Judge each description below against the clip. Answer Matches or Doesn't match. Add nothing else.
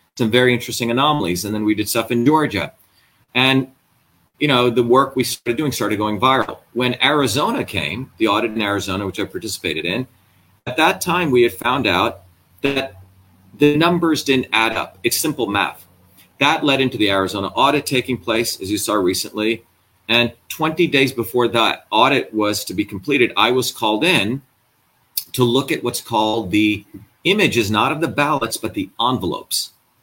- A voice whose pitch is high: Doesn't match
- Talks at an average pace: Matches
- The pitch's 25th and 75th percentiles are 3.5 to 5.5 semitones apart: Matches